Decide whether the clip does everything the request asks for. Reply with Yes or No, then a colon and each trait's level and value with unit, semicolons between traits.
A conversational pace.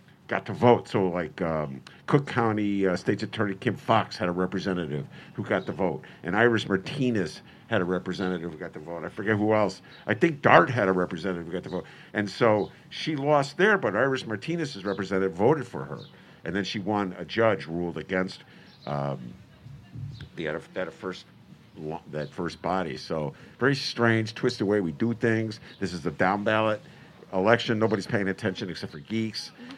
Yes: average, 185 wpm